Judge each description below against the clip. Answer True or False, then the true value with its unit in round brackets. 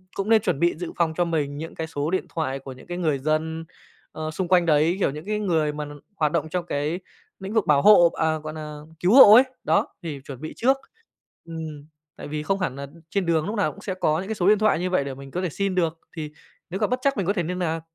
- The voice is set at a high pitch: False (165 Hz)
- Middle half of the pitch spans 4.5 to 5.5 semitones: False (3.6 semitones)